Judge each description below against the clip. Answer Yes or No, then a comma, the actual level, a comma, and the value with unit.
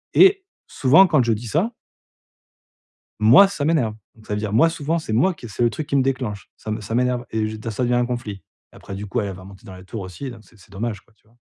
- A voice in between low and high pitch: No, low, 115 Hz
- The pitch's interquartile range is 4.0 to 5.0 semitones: Yes, average, 4.6 semitones